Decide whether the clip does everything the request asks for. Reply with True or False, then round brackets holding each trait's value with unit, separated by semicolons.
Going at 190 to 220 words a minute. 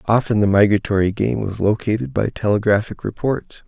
False (145 wpm)